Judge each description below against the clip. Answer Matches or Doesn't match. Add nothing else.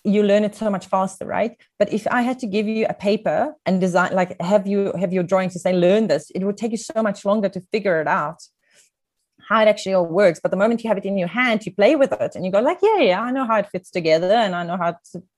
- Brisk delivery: Matches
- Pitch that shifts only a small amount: Doesn't match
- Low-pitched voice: Doesn't match